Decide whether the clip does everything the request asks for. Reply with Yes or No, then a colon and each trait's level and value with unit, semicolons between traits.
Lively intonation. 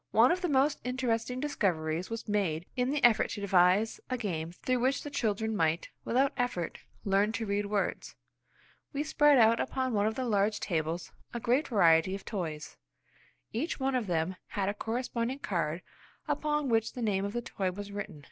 No: average, 5.0 semitones